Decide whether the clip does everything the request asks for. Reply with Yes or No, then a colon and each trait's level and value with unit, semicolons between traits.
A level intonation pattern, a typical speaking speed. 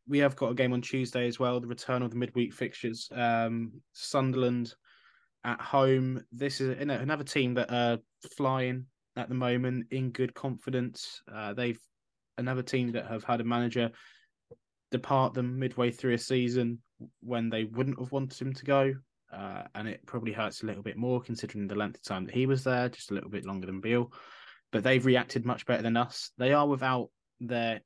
Yes: narrow, 1.8 semitones; average, 195 wpm